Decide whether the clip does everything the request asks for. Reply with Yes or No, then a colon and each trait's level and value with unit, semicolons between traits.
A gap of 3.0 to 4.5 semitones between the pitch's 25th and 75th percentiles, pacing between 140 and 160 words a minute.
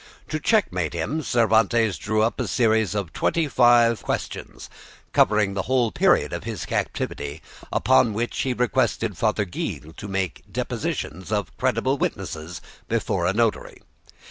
Yes: average, 4.0 semitones; average, 145 wpm